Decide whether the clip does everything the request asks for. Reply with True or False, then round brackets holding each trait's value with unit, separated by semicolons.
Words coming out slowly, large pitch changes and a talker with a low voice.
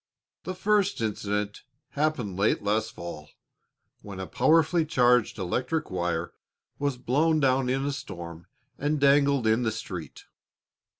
True (130 wpm; 6.1 semitones; 125 Hz)